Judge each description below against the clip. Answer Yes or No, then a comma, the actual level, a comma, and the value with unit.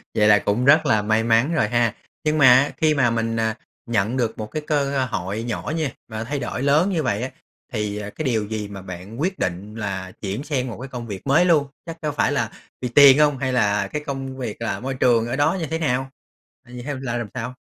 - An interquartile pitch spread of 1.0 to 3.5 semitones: No, average, 4.6 semitones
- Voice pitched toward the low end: Yes, low, 125 Hz